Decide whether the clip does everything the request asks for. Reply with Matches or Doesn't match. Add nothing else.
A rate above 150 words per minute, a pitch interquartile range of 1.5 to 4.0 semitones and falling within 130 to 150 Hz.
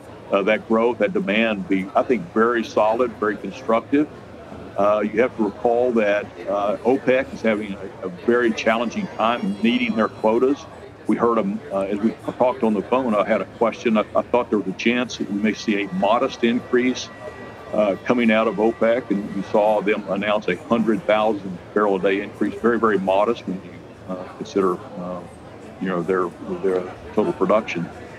Doesn't match